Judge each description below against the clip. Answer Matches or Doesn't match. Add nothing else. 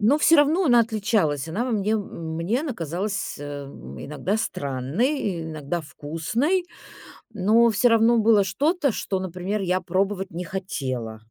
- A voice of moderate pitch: Doesn't match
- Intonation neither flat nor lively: Doesn't match